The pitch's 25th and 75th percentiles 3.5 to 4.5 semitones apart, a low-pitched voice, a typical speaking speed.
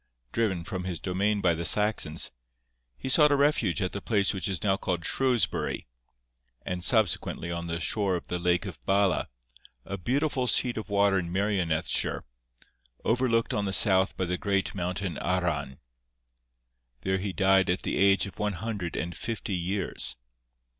No: average, 2.9 semitones; very low, 95 Hz; average, 165 wpm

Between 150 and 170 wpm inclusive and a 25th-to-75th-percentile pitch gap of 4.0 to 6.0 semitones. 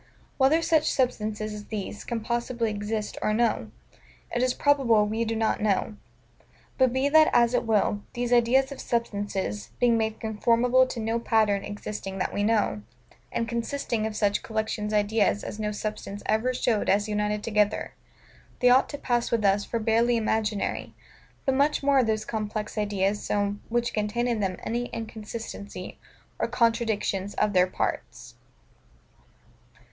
No: average, 160 wpm; narrow, 2.4 semitones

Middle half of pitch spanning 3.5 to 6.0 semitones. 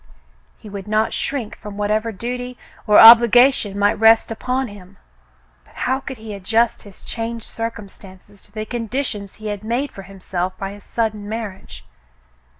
No: narrow, 2.5 semitones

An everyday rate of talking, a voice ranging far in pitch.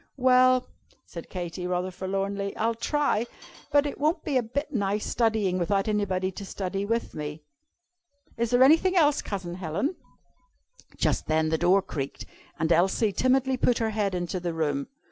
Yes: average, 165 wpm; wide, 5.9 semitones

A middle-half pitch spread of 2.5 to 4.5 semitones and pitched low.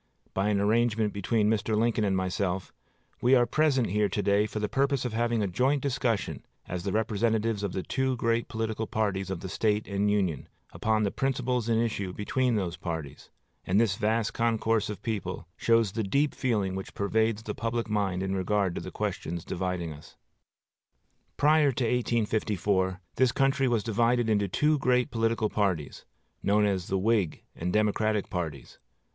Yes: average, 3.1 semitones; low, 105 Hz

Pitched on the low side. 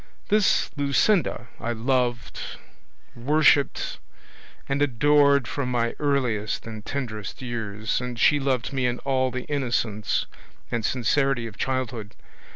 Yes: low, 125 Hz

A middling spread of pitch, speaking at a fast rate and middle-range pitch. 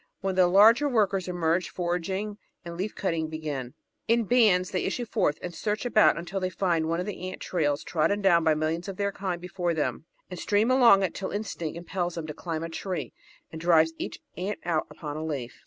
Yes: average, 3.4 semitones; fast, 210 wpm; medium, 180 Hz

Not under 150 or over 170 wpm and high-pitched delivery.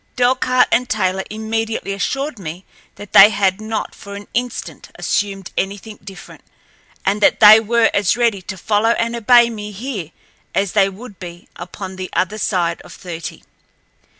Yes: average, 160 wpm; high, 205 Hz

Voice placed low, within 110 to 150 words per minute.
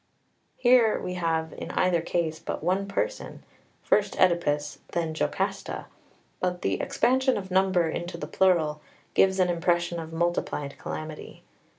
No: medium, 175 Hz; slow, 135 wpm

